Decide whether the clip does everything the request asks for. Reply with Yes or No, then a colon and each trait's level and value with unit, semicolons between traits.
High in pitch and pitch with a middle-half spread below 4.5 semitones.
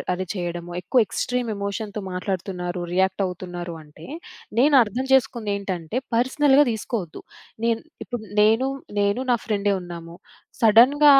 No: high, 200 Hz; average, 5.0 semitones